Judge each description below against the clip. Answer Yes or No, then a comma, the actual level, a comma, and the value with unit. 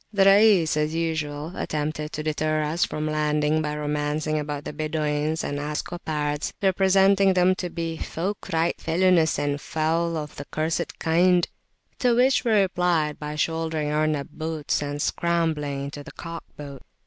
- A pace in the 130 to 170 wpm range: Yes, average, 160 wpm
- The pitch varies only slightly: Yes, narrow, 2.3 semitones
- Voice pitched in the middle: Yes, medium, 155 Hz